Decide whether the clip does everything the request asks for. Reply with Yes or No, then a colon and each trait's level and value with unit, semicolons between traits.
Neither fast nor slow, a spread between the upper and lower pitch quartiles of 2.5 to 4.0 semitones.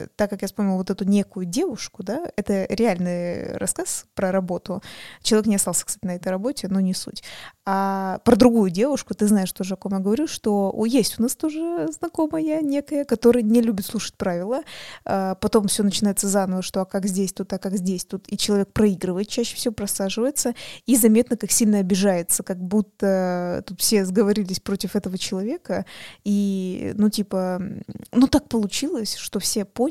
No: fast, 180 wpm; average, 3.3 semitones